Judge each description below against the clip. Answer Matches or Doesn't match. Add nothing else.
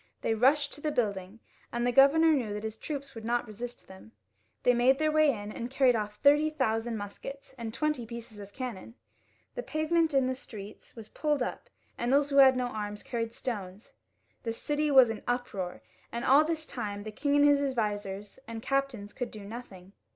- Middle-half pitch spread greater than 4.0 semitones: Matches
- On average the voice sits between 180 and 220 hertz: Doesn't match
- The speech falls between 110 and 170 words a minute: Doesn't match